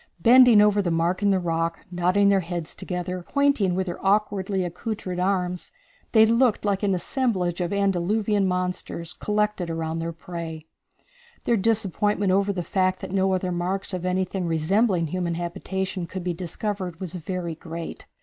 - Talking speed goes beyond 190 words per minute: No, average, 160 wpm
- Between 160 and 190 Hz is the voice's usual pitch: Yes, medium, 185 Hz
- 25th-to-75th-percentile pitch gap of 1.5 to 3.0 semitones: Yes, narrow, 2.6 semitones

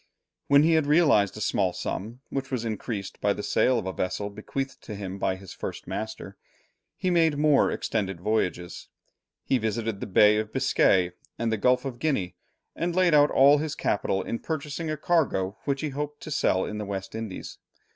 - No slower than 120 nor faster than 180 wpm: No, average, 195 wpm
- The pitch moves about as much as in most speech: No, wide, 6.5 semitones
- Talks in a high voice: No, low, 115 Hz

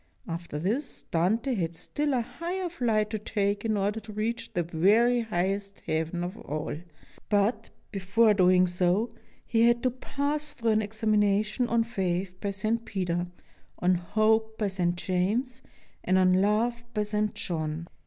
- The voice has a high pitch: Yes, high, 210 Hz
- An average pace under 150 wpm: No, average, 160 wpm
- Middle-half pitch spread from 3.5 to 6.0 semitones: Yes, average, 3.9 semitones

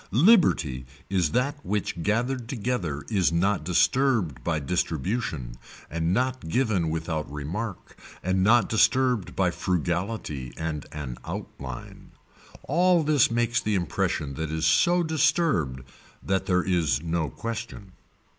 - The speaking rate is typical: No, slow, 125 wpm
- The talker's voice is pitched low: Yes, very low, 90 Hz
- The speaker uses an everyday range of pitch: No, wide, 7.0 semitones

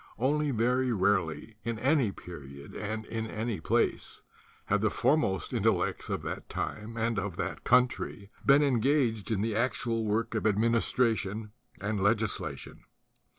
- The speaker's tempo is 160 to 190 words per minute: No, slow, 135 wpm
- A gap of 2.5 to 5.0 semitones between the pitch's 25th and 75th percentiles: Yes, average, 3.0 semitones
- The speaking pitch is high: No, low, 110 Hz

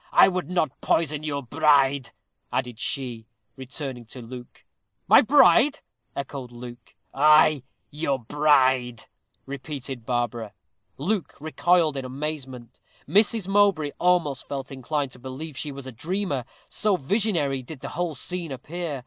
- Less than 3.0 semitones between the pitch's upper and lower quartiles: No, average, 4.2 semitones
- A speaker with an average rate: No, slow, 130 wpm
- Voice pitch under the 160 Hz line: Yes, medium, 140 Hz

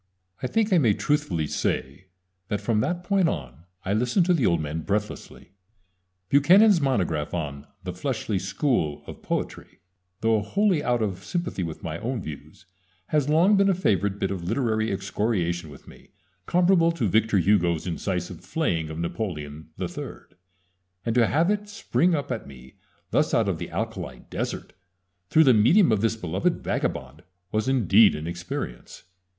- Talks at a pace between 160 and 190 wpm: Yes, average, 165 wpm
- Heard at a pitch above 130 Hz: No, low, 110 Hz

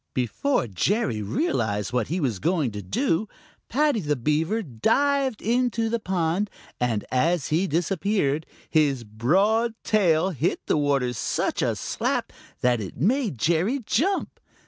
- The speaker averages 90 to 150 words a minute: Yes, average, 140 wpm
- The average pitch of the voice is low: No, medium, 165 Hz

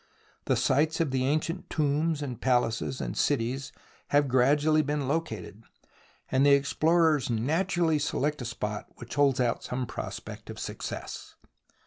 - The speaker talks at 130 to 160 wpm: Yes, average, 140 wpm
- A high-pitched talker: No, medium, 140 Hz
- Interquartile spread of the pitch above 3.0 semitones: Yes, average, 3.8 semitones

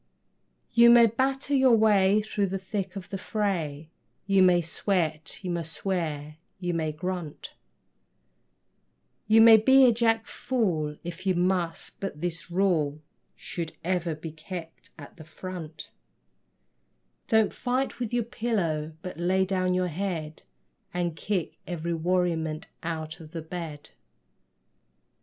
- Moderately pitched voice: Yes, medium, 180 Hz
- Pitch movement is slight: No, average, 4.1 semitones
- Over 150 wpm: No, slow, 135 wpm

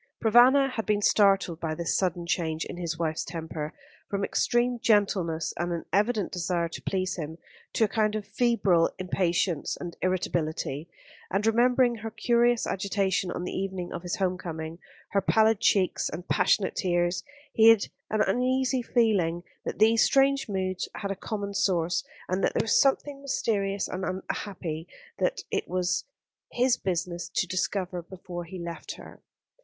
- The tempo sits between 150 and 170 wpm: Yes, average, 160 wpm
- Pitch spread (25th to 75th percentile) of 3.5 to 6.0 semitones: Yes, average, 4.1 semitones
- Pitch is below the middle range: No, high, 190 Hz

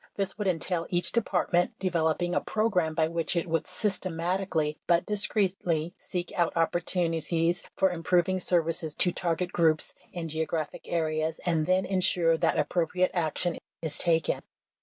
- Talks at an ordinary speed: Yes, average, 150 wpm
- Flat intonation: Yes, narrow, 2.1 semitones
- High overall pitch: No, medium, 175 Hz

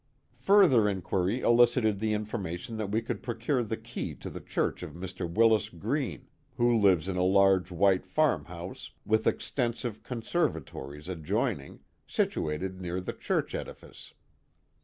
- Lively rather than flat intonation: No, average, 4.4 semitones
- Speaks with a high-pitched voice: No, low, 105 Hz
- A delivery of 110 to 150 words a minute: Yes, average, 140 wpm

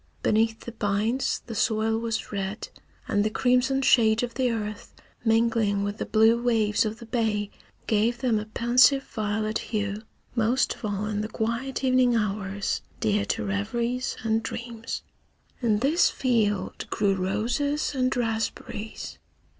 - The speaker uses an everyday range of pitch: No, narrow, 2.3 semitones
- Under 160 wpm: Yes, average, 145 wpm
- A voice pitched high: Yes, high, 225 Hz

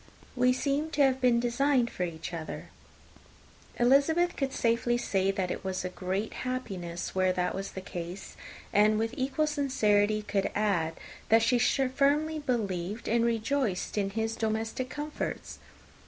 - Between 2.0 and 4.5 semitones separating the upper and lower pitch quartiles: No, average, 5.2 semitones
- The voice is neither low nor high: No, high, 225 Hz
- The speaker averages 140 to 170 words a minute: Yes, average, 150 wpm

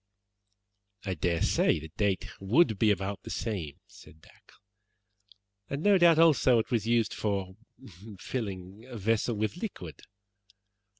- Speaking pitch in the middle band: No, low, 105 Hz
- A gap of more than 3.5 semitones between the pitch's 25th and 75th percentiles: Yes, average, 4.5 semitones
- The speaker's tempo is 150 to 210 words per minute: No, slow, 135 wpm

